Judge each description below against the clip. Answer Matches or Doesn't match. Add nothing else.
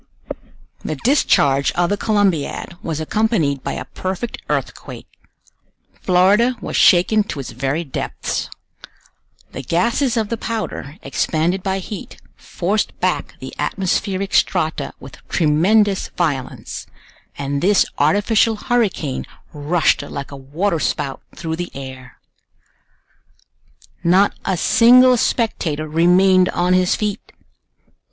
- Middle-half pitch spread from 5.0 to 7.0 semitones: Matches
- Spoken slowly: Matches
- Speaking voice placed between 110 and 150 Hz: Doesn't match